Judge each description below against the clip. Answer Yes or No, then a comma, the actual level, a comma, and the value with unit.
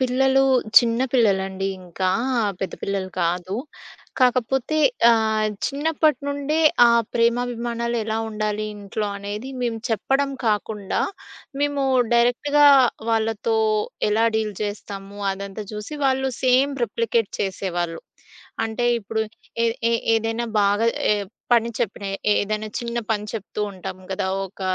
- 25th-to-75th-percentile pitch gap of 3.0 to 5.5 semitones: Yes, average, 3.3 semitones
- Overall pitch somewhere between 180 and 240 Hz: Yes, high, 225 Hz